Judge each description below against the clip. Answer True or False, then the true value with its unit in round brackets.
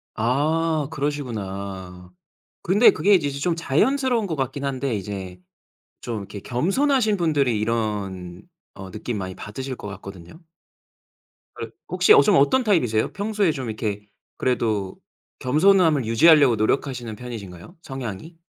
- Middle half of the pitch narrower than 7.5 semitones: False (7.8 semitones)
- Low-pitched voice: True (130 Hz)